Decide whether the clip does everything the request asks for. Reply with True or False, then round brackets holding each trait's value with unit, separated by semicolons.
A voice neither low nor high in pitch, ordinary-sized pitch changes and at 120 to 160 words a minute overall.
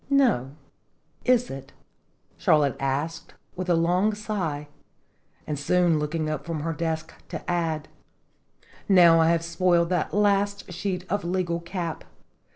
True (170 Hz; 3.0 semitones; 135 wpm)